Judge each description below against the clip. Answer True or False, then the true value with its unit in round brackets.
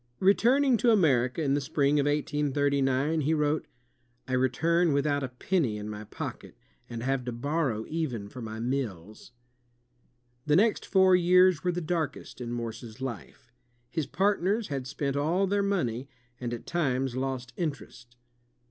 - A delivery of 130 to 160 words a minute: True (155 wpm)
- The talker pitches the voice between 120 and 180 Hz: True (140 Hz)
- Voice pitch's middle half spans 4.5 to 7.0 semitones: True (5.4 semitones)